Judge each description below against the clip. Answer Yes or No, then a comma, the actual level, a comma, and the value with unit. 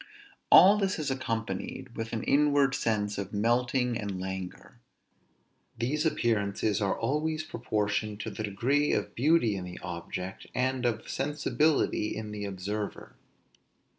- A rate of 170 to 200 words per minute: No, slow, 135 wpm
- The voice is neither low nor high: No, low, 115 Hz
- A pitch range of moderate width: Yes, average, 5.0 semitones